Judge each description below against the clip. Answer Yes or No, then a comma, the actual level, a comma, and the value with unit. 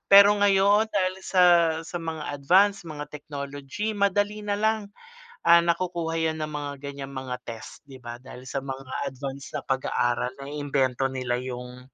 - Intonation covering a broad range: Yes, wide, 6.3 semitones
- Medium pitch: Yes, medium, 145 Hz